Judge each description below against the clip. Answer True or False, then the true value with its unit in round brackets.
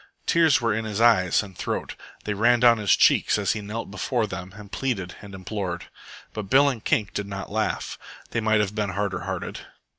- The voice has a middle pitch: False (105 Hz)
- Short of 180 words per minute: False (205 wpm)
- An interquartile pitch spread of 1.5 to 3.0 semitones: True (2.7 semitones)